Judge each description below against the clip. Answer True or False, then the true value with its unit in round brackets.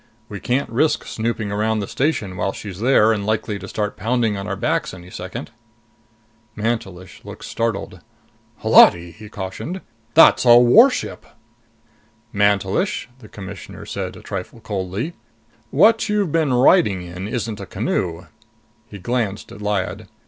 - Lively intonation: False (3.9 semitones)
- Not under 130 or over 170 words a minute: True (140 wpm)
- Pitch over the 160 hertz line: False (105 Hz)